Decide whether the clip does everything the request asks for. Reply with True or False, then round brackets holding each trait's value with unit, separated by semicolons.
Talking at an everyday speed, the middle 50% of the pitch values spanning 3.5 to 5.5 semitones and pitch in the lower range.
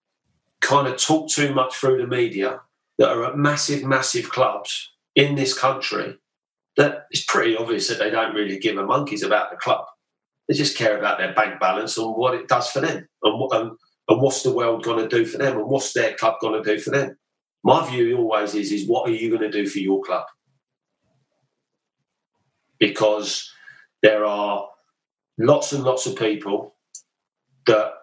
True (180 wpm; 4.6 semitones; 130 Hz)